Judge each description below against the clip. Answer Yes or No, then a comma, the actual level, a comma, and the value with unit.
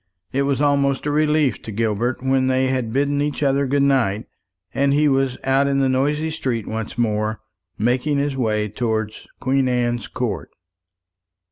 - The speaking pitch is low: Yes, low, 130 Hz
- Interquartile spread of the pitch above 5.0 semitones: No, average, 3.4 semitones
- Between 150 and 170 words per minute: Yes, average, 165 wpm